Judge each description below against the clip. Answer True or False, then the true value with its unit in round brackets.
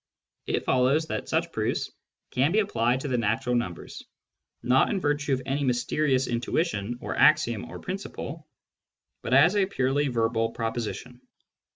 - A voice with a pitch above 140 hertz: False (130 Hz)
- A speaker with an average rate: True (150 wpm)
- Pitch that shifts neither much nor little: True (4.3 semitones)